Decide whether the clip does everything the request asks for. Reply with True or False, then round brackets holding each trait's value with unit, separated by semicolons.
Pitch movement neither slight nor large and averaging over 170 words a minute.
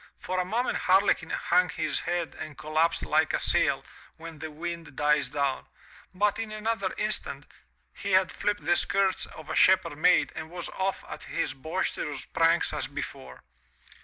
False (3.4 semitones; 165 wpm)